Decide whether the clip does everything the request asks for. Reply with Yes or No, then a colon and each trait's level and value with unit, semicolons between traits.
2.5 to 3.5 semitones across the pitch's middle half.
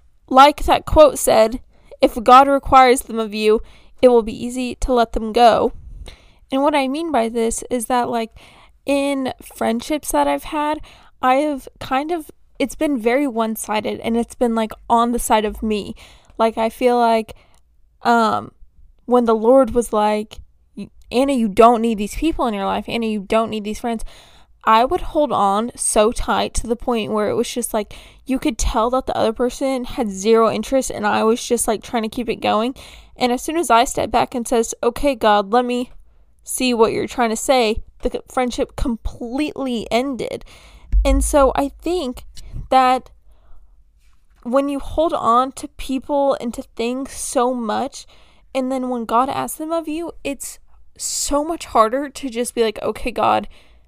Yes: average, 3.1 semitones